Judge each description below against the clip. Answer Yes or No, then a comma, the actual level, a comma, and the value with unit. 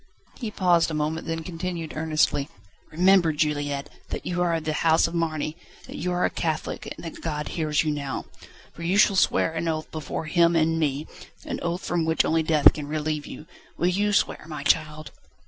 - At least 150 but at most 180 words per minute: No, average, 200 wpm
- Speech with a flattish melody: Yes, narrow, 1.8 semitones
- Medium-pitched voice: Yes, medium, 160 Hz